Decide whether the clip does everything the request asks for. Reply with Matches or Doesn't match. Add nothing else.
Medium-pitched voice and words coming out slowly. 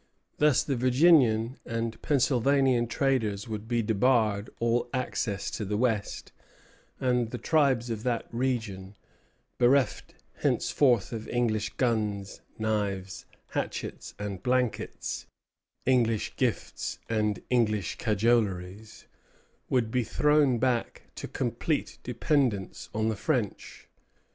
Doesn't match